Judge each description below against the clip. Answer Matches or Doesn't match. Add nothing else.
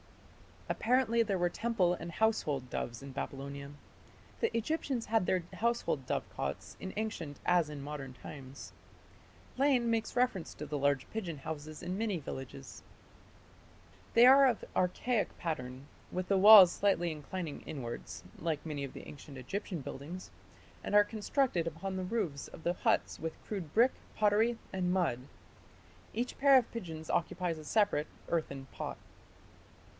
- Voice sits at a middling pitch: Matches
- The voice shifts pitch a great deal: Matches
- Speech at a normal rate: Matches